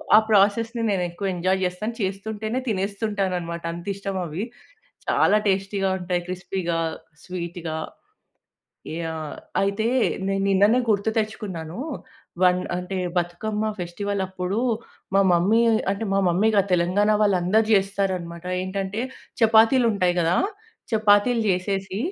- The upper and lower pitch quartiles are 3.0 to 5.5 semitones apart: No, narrow, 2.5 semitones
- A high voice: Yes, high, 195 Hz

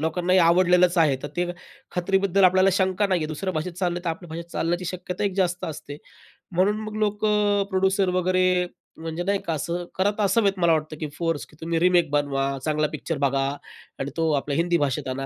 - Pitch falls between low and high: Yes, medium, 175 Hz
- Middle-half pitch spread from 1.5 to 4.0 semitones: Yes, average, 2.9 semitones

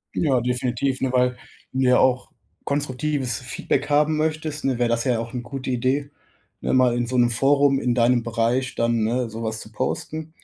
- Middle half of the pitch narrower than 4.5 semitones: Yes, average, 2.7 semitones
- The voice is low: Yes, low, 125 Hz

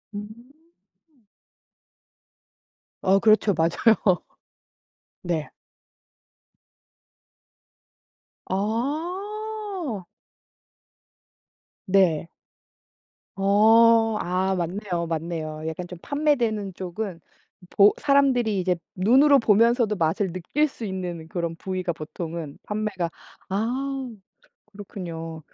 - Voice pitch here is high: Yes, high, 200 Hz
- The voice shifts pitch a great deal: No, average, 5.0 semitones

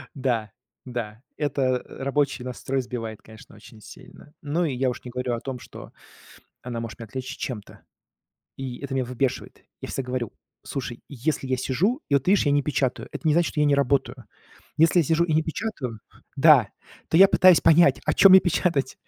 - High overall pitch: No, low, 135 Hz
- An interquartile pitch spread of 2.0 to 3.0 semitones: No, average, 3.7 semitones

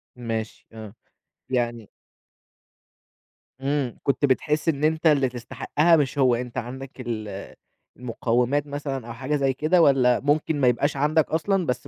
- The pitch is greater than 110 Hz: Yes, low, 135 Hz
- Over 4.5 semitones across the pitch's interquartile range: No, average, 3.4 semitones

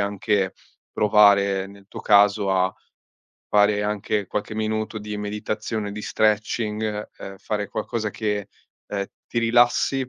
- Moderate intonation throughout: No, narrow, 1.2 semitones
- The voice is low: Yes, low, 105 Hz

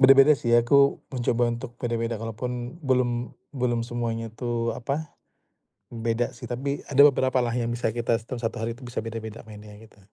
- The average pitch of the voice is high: No, low, 120 Hz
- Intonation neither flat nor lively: No, narrow, 1.9 semitones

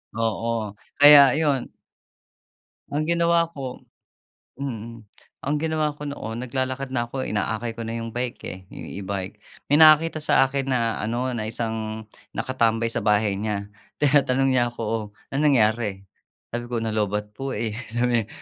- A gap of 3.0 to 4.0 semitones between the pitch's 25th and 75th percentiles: Yes, average, 3.7 semitones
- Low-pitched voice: Yes, low, 120 Hz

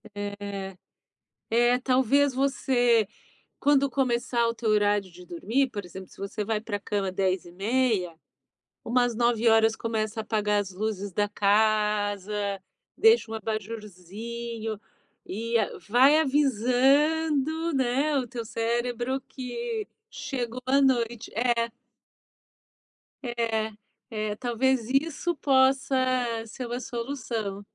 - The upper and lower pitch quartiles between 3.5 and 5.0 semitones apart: Yes, average, 3.9 semitones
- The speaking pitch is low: No, high, 235 Hz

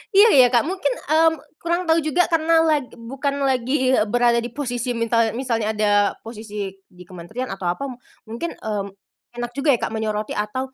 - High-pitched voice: Yes, high, 245 Hz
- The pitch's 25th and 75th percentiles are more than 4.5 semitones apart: Yes, average, 4.9 semitones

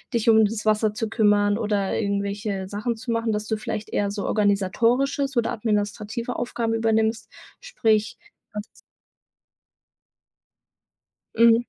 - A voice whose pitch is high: Yes, high, 220 Hz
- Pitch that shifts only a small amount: Yes, narrow, 2.0 semitones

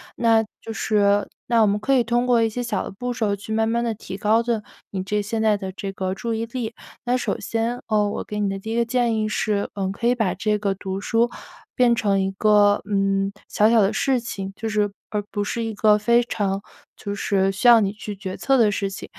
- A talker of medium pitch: No, high, 215 Hz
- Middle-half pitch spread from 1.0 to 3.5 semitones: Yes, narrow, 2.4 semitones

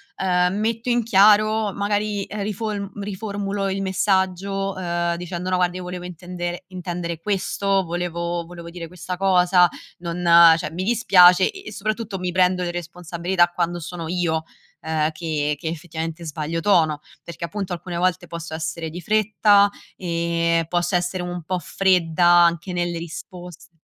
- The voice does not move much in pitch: Yes, narrow, 2.3 semitones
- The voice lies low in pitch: No, medium, 180 Hz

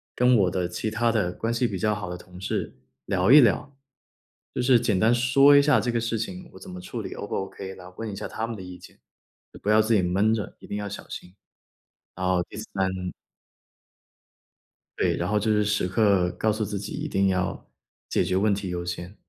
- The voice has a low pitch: Yes, low, 105 Hz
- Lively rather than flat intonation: No, average, 3.6 semitones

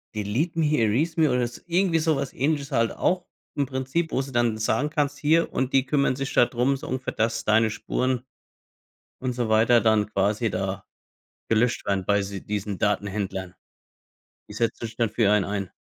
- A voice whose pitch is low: Yes, low, 120 Hz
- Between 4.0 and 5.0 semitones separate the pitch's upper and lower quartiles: Yes, average, 4.7 semitones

